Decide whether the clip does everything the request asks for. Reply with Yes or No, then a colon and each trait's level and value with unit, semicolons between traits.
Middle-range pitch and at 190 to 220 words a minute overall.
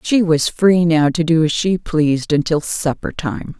Yes: medium, 160 Hz; average, 200 wpm